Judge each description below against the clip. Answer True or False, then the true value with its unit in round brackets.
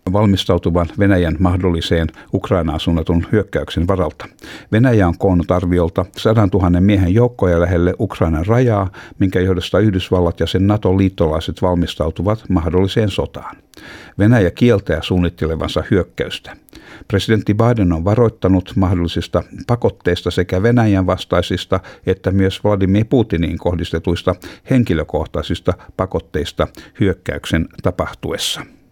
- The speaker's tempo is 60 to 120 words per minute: True (100 wpm)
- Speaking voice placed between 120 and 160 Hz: False (95 Hz)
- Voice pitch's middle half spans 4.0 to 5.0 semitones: False (3.0 semitones)